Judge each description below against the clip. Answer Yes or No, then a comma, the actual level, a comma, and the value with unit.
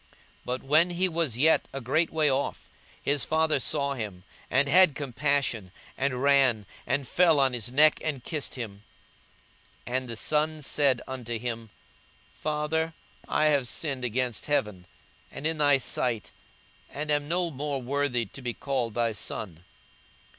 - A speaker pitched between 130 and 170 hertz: Yes, low, 135 Hz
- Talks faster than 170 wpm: No, average, 155 wpm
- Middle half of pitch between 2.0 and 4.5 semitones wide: Yes, average, 3.8 semitones